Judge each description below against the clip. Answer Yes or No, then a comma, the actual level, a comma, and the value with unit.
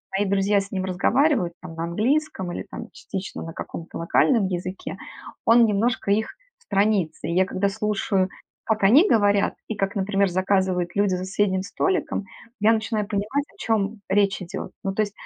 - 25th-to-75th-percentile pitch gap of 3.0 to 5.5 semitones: No, narrow, 2.4 semitones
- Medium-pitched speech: No, high, 200 Hz